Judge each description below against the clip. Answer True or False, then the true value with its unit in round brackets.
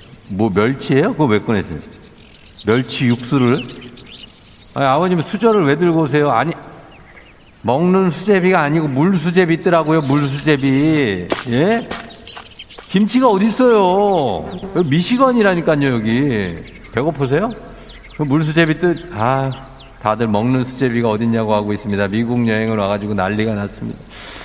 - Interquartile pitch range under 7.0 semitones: False (7.3 semitones)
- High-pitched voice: False (140 Hz)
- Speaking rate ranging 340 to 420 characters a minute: False (290 characters per minute)